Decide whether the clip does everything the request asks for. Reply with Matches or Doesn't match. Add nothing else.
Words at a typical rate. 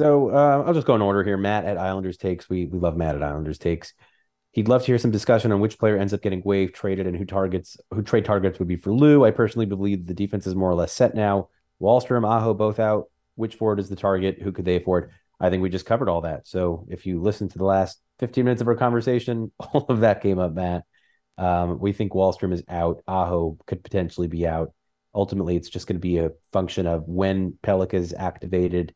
Doesn't match